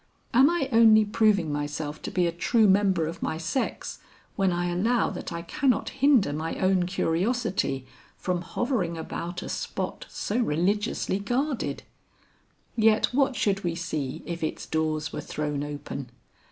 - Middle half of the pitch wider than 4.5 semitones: Yes, wide, 5.6 semitones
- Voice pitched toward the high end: No, medium, 180 Hz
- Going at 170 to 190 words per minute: No, average, 155 wpm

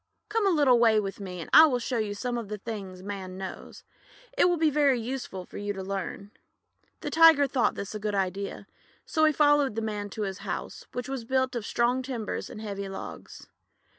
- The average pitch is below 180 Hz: No, high, 225 Hz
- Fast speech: Yes, fast, 215 wpm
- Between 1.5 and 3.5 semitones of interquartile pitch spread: No, average, 5.1 semitones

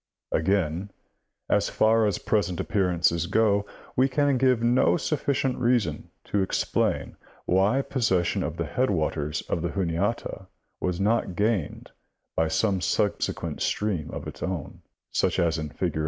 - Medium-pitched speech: No, low, 100 Hz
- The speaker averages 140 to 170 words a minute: Yes, average, 145 wpm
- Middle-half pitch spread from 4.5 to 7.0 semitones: Yes, average, 5.1 semitones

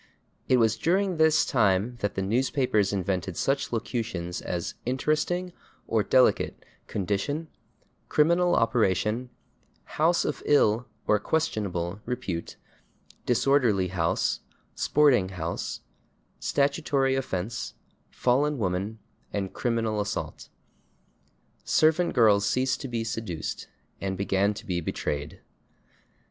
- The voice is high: No, low, 115 Hz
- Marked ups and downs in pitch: Yes, wide, 6.0 semitones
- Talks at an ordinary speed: No, slow, 105 wpm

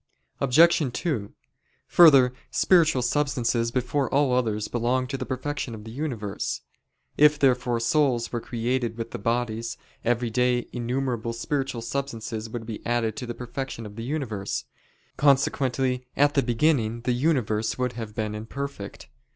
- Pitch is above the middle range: No, low, 125 Hz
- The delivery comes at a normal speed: Yes, average, 145 wpm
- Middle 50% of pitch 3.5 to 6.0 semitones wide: No, average, 2.9 semitones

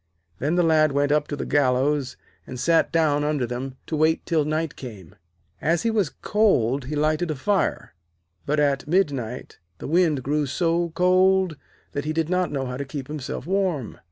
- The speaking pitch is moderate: Yes, medium, 150 Hz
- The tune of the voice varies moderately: Yes, average, 3.6 semitones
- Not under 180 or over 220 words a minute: Yes, average, 185 wpm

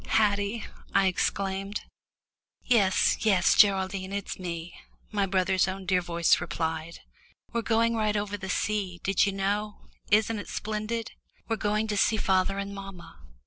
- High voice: Yes, high, 195 Hz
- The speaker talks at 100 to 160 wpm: Yes, average, 145 wpm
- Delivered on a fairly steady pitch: Yes, narrow, 2.1 semitones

